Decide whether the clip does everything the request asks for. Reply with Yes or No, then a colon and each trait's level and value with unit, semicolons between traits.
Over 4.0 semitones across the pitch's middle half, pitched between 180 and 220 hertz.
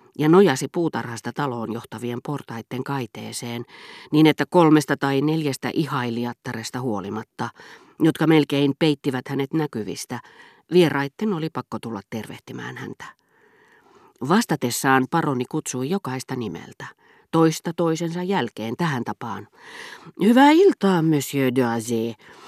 No: average, 5.2 semitones; medium, 140 Hz